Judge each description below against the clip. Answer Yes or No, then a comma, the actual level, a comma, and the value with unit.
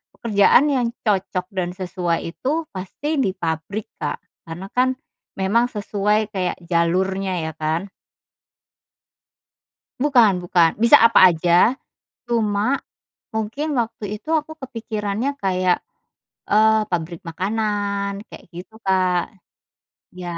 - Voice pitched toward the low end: No, high, 200 Hz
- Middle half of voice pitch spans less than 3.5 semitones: No, average, 3.8 semitones